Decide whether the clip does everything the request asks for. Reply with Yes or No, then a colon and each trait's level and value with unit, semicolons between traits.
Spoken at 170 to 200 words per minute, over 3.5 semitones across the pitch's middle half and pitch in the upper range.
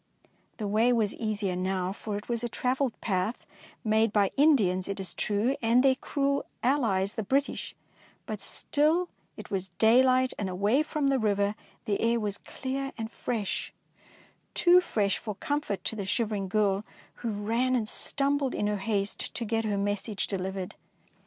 Yes: average, 175 wpm; average, 4.3 semitones; high, 220 Hz